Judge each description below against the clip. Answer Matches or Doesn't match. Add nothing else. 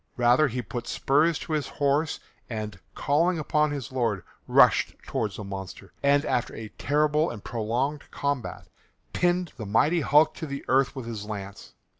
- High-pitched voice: Doesn't match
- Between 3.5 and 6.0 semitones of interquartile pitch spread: Matches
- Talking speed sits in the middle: Matches